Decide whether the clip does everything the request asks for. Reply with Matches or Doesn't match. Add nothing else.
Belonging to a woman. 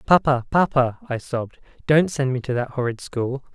Doesn't match